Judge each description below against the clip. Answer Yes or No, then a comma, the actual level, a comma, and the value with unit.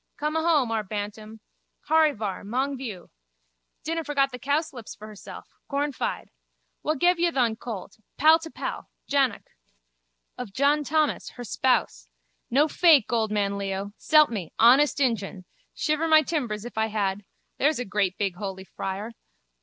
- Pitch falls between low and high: No, high, 245 Hz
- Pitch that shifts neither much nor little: No, wide, 6.3 semitones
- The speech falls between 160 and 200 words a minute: No, average, 150 wpm